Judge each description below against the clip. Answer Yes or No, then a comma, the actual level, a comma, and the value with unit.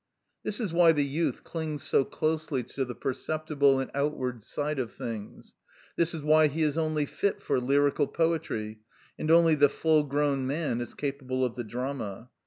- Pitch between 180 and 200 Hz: No, medium, 145 Hz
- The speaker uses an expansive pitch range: No, average, 3.3 semitones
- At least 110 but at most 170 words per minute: No, average, 180 wpm